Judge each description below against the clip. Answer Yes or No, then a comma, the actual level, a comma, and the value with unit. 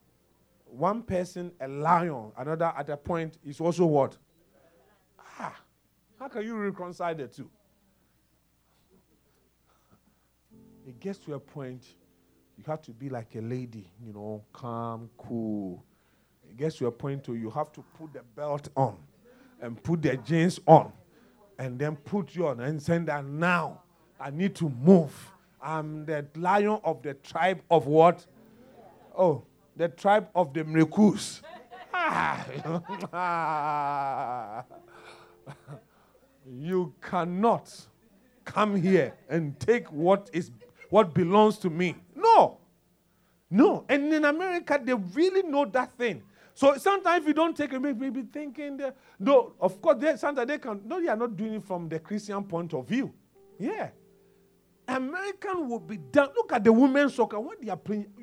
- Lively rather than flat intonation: Yes, wide, 7.0 semitones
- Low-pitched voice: No, medium, 175 Hz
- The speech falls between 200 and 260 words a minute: No, average, 150 wpm